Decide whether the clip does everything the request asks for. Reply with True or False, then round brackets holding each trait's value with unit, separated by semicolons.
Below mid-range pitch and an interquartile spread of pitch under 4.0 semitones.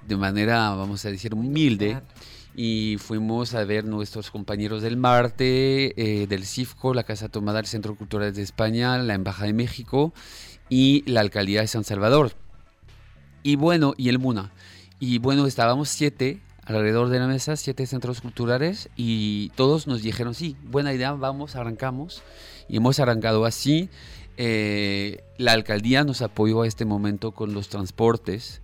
True (115 Hz; 3.6 semitones)